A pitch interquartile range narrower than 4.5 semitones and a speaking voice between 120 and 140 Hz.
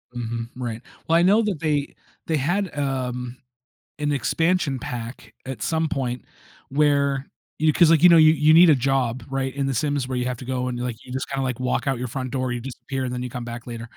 Yes: average, 3.2 semitones; low, 135 Hz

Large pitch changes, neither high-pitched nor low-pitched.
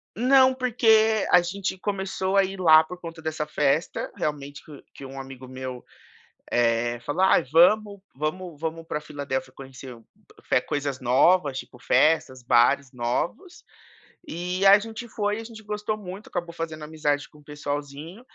Yes: wide, 6.0 semitones; medium, 160 Hz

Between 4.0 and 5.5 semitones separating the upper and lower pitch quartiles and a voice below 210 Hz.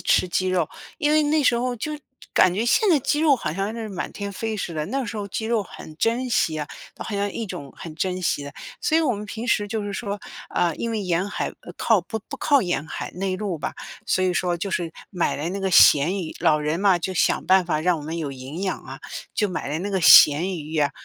Yes: average, 4.8 semitones; high, 190 Hz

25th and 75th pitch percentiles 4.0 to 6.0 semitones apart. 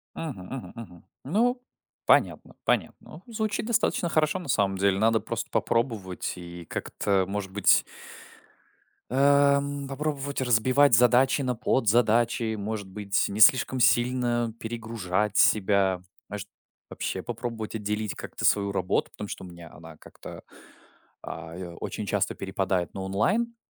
Yes: average, 5.2 semitones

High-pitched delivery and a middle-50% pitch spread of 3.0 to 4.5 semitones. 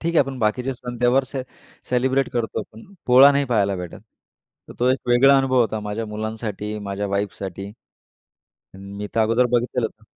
No: low, 115 Hz; average, 3.5 semitones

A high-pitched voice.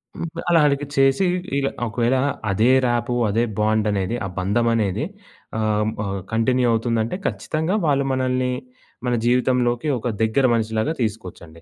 No: low, 120 Hz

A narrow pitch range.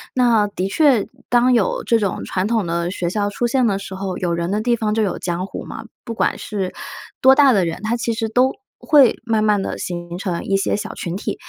No: average, 4.2 semitones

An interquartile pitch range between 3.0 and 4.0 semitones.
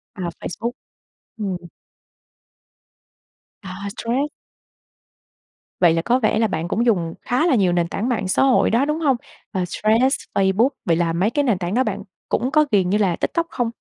No: wide, 5.5 semitones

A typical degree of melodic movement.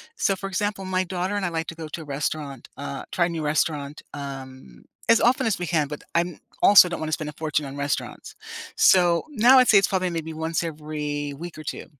Yes: average, 3.8 semitones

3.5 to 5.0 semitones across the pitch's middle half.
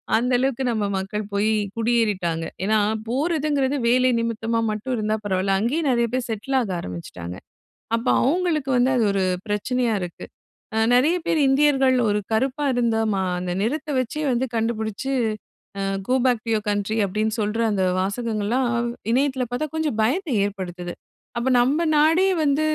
Yes: average, 4.2 semitones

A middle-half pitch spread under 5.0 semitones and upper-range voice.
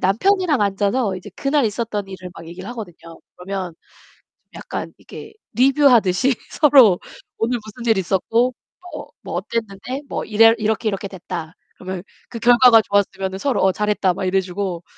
Yes: average, 4.1 semitones; high, 205 Hz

